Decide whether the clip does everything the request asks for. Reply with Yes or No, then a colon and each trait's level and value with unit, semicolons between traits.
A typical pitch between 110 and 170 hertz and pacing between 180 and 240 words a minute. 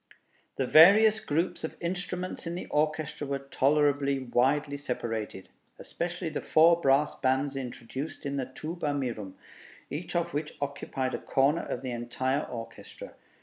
No: medium, 140 Hz; average, 145 wpm